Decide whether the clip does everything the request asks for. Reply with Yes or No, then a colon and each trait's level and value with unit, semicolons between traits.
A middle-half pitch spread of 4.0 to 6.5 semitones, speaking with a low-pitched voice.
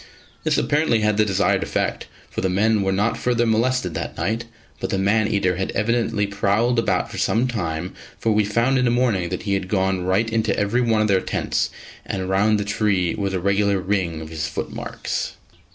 No: average, 3.0 semitones; low, 105 Hz